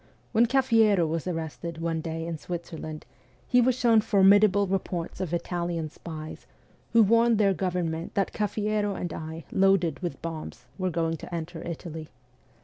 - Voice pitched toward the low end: No, medium, 175 Hz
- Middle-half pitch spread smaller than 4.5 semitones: Yes, average, 3.9 semitones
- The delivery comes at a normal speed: Yes, average, 150 wpm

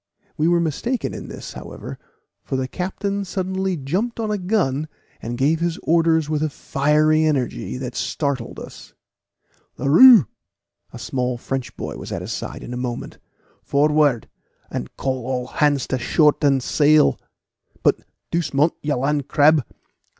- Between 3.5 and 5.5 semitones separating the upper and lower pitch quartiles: Yes, average, 4.1 semitones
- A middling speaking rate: Yes, average, 150 wpm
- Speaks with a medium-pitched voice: Yes, medium, 150 Hz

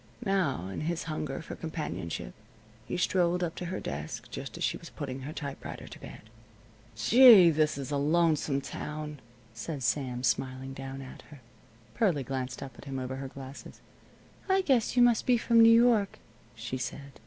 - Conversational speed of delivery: Yes, average, 180 wpm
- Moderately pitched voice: Yes, medium, 145 Hz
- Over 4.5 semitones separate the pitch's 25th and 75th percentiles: Yes, average, 5.2 semitones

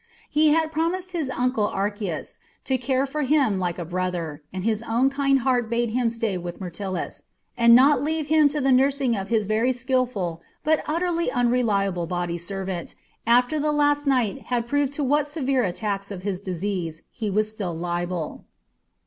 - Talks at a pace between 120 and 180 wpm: Yes, average, 175 wpm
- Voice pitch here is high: Yes, high, 235 Hz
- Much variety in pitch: Yes, wide, 6.4 semitones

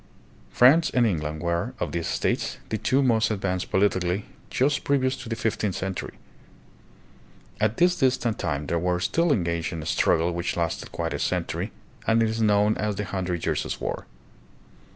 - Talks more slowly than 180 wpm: Yes, average, 170 wpm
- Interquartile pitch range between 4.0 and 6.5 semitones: Yes, average, 5.0 semitones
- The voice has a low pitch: Yes, low, 100 Hz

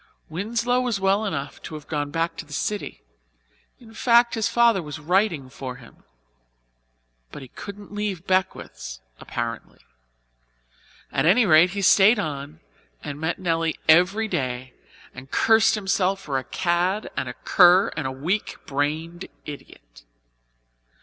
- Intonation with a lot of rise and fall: Yes, wide, 5.9 semitones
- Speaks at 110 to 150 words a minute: Yes, average, 145 wpm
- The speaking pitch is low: No, medium, 175 Hz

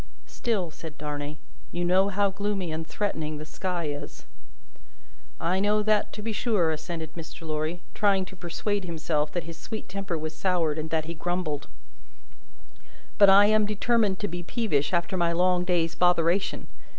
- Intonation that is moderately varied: Yes, average, 3.7 semitones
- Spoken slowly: No, average, 165 wpm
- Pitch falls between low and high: Yes, medium, 175 Hz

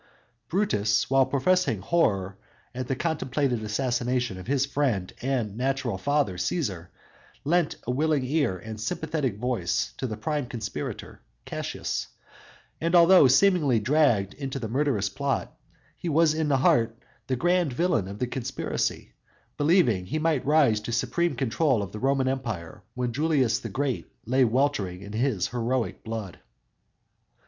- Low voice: Yes, low, 130 Hz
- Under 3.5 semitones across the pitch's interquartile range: No, average, 4.9 semitones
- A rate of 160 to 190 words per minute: No, average, 145 wpm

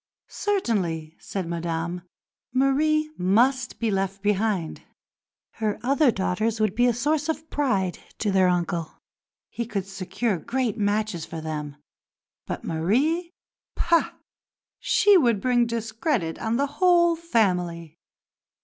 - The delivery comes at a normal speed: No, slow, 120 wpm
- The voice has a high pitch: Yes, high, 220 Hz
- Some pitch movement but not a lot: No, wide, 6.8 semitones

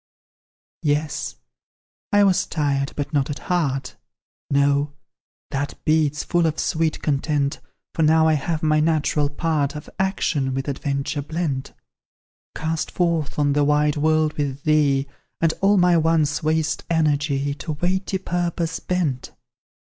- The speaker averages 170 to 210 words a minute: No, slow, 135 wpm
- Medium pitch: Yes, medium, 155 Hz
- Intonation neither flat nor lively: No, narrow, 2.3 semitones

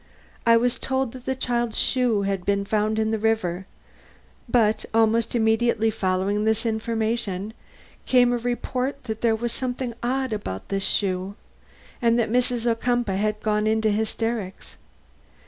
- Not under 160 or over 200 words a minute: No, average, 145 wpm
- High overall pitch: Yes, high, 225 Hz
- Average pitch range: No, narrow, 2.3 semitones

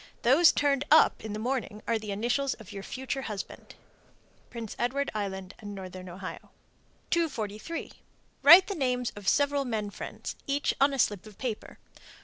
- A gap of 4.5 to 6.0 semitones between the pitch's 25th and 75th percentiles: Yes, average, 5.2 semitones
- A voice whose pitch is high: Yes, high, 235 Hz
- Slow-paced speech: No, average, 160 wpm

